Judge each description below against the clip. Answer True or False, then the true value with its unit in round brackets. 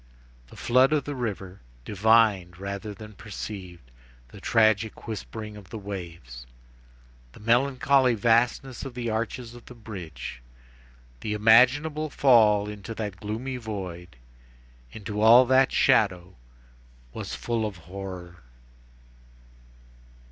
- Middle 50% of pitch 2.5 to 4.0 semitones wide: True (3.7 semitones)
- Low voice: True (110 Hz)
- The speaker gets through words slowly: True (115 wpm)